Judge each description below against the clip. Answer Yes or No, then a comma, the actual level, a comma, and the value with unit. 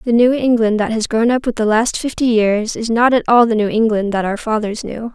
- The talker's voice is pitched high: Yes, high, 225 Hz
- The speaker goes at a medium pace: No, fast, 270 wpm